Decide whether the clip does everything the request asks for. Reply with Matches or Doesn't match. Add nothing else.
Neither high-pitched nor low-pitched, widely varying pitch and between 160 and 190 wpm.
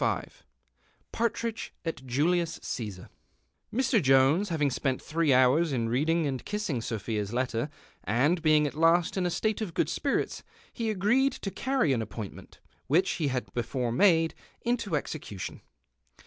Doesn't match